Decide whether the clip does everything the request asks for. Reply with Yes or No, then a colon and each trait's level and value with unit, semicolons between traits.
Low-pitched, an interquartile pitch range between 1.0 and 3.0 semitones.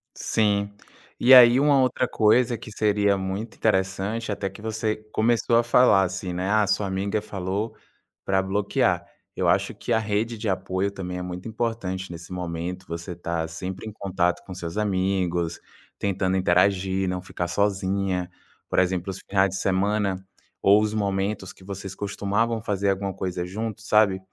Yes: low, 100 Hz; narrow, 2.4 semitones